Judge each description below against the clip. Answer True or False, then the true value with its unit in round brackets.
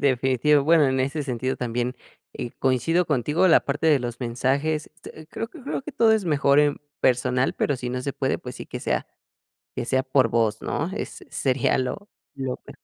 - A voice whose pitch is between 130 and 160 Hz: True (135 Hz)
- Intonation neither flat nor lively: True (3.3 semitones)